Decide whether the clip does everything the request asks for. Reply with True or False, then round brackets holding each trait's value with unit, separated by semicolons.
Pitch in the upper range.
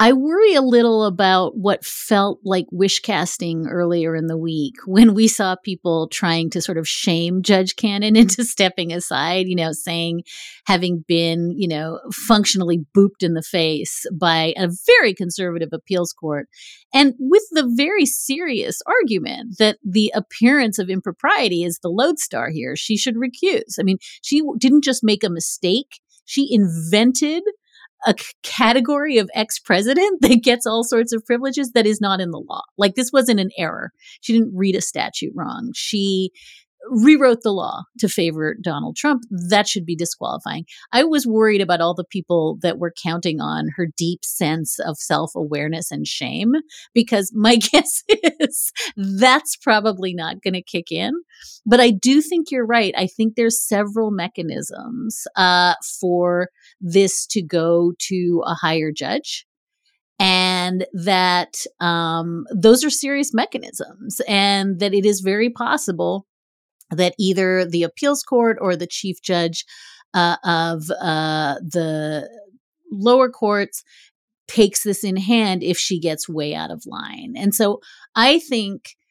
True (200 Hz)